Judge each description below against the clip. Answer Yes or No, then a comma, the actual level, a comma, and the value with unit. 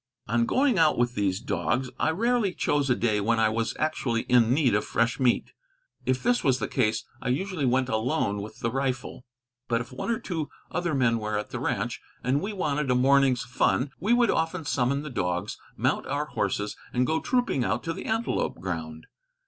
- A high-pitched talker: No, low, 130 Hz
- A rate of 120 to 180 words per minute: No, fast, 205 wpm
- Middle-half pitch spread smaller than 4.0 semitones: No, average, 5.3 semitones